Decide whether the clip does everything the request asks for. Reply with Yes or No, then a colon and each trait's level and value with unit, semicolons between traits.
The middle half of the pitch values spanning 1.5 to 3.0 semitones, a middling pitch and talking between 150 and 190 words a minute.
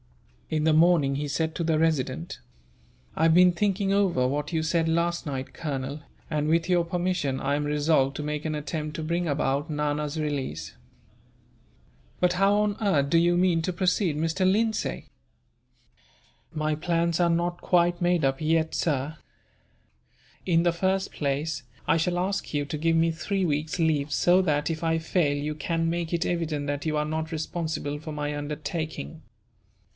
Yes: average, 2.7 semitones; medium, 160 Hz; average, 175 wpm